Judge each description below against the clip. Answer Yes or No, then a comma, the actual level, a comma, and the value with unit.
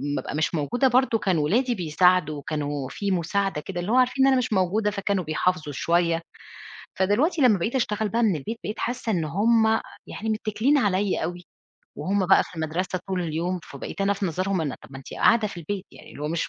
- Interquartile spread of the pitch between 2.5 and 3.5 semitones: No, average, 4.6 semitones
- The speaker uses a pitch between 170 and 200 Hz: Yes, high, 190 Hz